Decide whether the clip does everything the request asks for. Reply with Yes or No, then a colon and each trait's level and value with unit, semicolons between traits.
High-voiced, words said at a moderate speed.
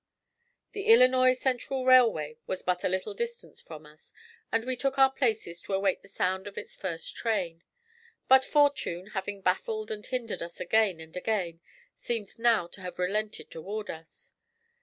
Yes: high, 210 Hz; average, 165 wpm